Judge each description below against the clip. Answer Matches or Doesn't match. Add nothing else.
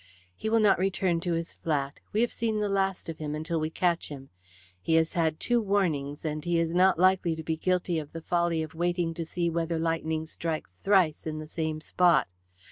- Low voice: Doesn't match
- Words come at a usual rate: Doesn't match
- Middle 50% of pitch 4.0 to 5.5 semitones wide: Doesn't match